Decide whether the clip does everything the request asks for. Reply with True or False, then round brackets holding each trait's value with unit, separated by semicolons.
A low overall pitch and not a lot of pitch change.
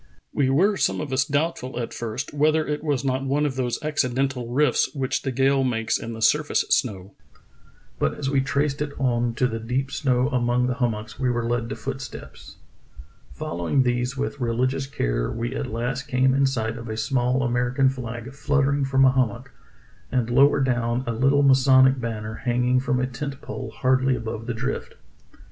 True (130 Hz; 2.3 semitones)